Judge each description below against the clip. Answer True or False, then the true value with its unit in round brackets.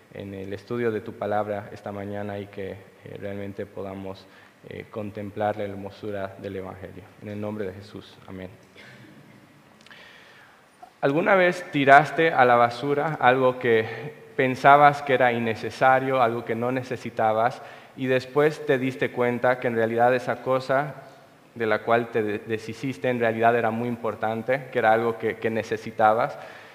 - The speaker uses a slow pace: False (145 wpm)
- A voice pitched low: True (115 Hz)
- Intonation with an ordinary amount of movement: True (3.8 semitones)